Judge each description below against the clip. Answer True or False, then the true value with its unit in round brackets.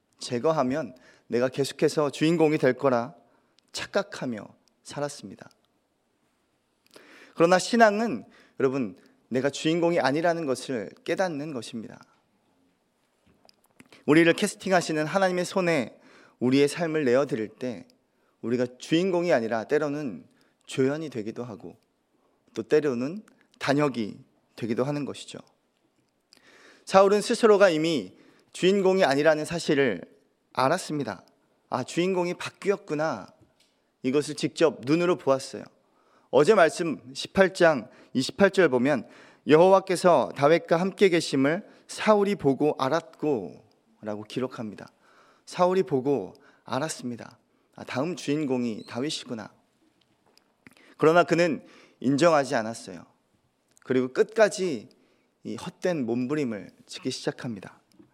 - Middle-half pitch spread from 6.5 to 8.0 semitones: False (5.5 semitones)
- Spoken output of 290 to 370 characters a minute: False (260 characters per minute)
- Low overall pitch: False (155 Hz)